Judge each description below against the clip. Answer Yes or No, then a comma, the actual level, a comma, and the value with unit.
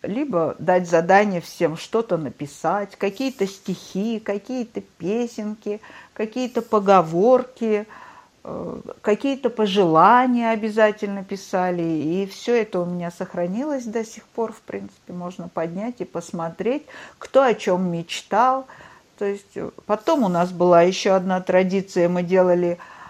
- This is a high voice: Yes, high, 200 Hz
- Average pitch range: Yes, average, 4.1 semitones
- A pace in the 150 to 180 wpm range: No, average, 120 wpm